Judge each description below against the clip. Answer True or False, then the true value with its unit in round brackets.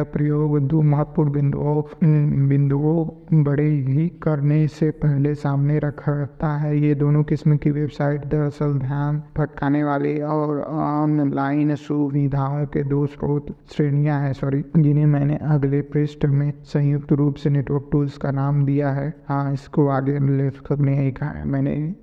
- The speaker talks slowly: False (140 wpm)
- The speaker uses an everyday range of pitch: False (1.1 semitones)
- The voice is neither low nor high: True (145 Hz)